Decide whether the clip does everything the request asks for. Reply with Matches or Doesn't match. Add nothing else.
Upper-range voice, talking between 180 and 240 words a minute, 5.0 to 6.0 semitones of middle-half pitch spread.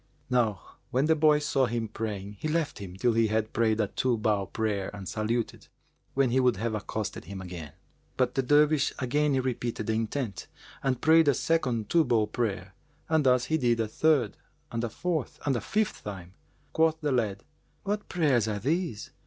Doesn't match